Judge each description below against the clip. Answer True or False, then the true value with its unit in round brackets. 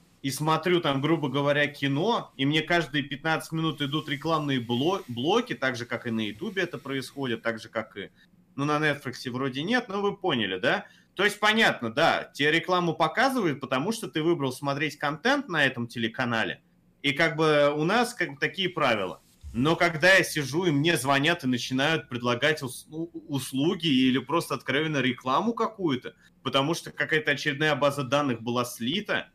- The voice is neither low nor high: True (145 Hz)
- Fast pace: True (175 wpm)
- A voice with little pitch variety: False (3.9 semitones)